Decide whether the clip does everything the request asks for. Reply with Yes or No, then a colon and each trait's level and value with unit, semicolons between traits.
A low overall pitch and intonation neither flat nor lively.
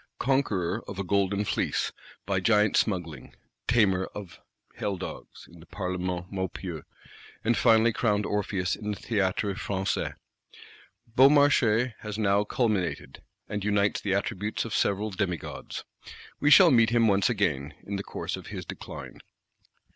Yes: low, 100 Hz; average, 3.0 semitones